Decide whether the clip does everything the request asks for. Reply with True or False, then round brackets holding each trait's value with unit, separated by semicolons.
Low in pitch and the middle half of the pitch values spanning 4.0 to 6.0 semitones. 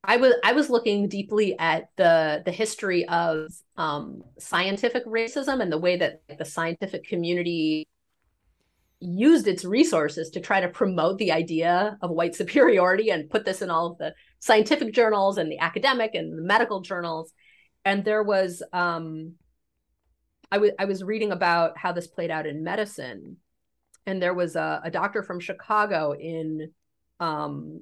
False (175 Hz; 4.5 semitones)